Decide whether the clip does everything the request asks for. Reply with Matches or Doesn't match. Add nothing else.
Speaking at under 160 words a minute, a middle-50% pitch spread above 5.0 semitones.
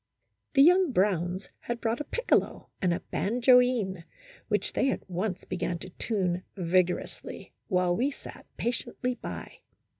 Matches